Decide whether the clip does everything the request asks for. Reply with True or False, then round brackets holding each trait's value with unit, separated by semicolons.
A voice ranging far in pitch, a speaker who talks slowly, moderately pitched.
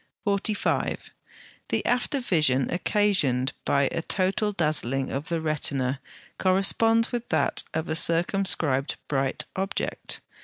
True (6.3 semitones; 115 wpm; 170 Hz)